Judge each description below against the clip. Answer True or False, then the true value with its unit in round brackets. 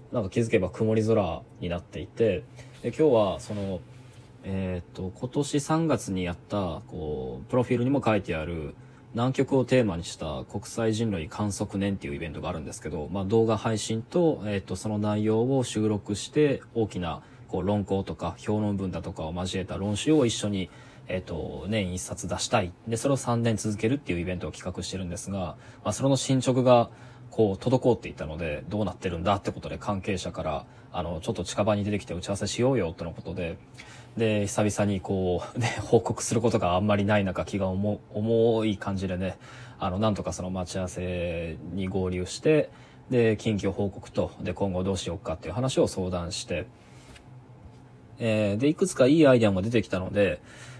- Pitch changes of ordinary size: True (4.5 semitones)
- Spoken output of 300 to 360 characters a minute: False (375 characters per minute)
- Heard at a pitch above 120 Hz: False (105 Hz)